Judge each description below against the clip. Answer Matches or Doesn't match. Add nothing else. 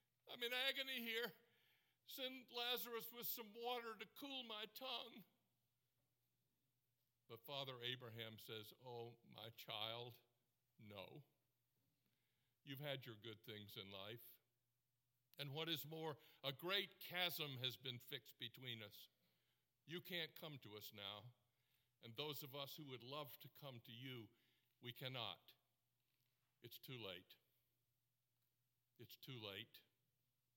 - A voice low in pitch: Matches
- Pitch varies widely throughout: Doesn't match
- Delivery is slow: Matches